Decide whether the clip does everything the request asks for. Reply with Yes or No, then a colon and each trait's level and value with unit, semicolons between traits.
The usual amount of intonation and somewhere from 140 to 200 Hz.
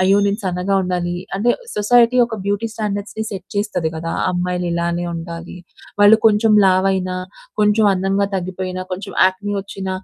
No: narrow, 2.3 semitones; high, 190 Hz